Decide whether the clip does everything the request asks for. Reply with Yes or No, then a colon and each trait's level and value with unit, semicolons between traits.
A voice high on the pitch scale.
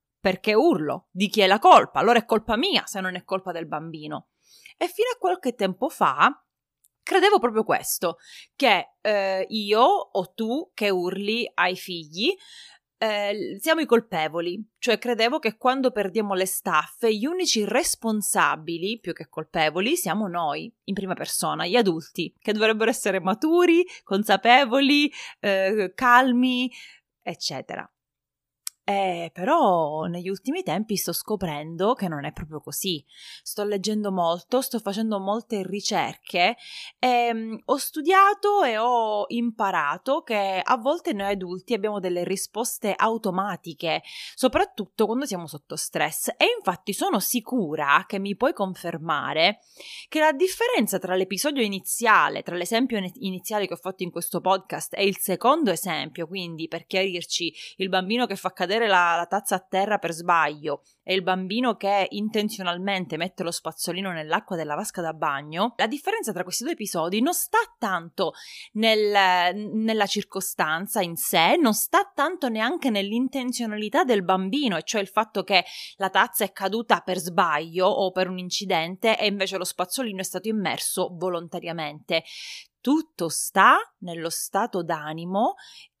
Yes: high, 200 Hz